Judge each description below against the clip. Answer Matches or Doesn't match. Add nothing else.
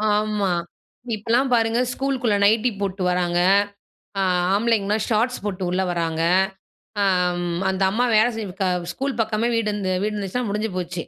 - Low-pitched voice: Doesn't match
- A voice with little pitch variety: Doesn't match